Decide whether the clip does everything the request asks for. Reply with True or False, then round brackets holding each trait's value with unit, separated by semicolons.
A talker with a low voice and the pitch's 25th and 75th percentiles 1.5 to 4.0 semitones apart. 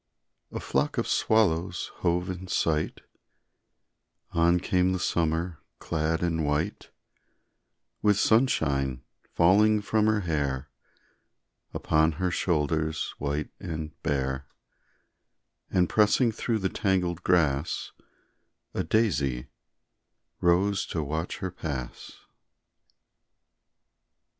True (85 Hz; 3.6 semitones)